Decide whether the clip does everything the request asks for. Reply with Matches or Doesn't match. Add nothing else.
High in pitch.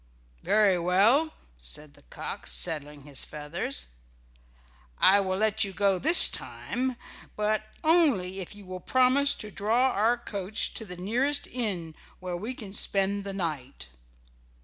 Matches